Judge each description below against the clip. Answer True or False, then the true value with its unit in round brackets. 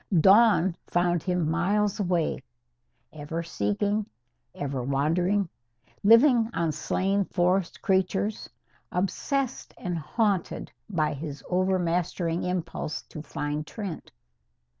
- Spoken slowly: True (95 wpm)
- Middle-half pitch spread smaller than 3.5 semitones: False (3.8 semitones)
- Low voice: False (180 Hz)